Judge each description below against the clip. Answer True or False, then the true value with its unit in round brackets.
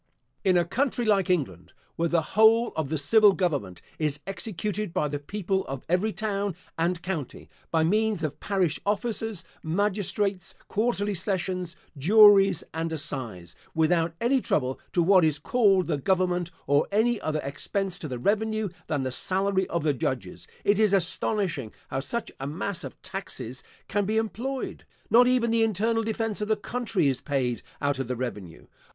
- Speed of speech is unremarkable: True (170 wpm)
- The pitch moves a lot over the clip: True (5.7 semitones)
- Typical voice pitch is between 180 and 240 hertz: True (185 Hz)